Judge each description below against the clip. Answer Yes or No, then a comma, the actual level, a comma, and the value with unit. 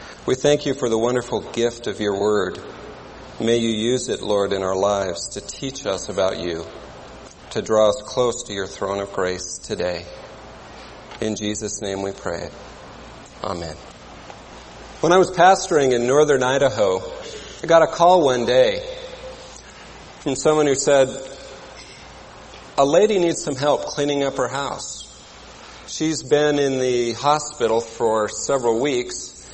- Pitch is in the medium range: No, low, 125 Hz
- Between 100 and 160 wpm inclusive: Yes, average, 150 wpm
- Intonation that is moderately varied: No, wide, 6.7 semitones